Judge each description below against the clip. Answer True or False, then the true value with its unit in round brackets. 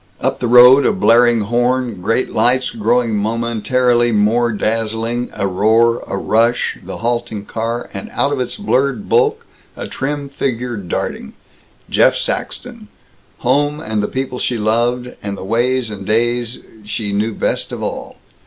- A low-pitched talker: True (120 Hz)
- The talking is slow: False (155 wpm)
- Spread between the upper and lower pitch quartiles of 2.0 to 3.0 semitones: True (2.5 semitones)